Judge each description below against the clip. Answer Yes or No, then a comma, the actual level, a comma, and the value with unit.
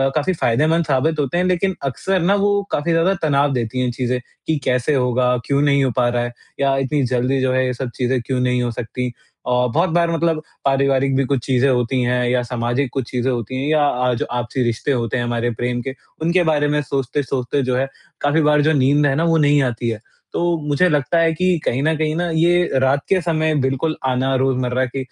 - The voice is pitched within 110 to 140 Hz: Yes, low, 135 Hz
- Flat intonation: No, average, 3.8 semitones